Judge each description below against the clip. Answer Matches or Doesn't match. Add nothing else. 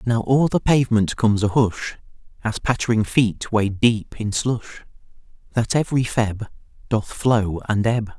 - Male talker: Matches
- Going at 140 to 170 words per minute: Matches